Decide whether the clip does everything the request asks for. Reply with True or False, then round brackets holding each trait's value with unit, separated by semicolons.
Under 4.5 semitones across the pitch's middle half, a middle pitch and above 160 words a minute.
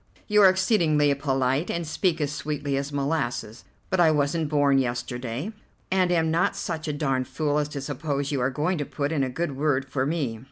True (3.0 semitones; 145 Hz; 205 wpm)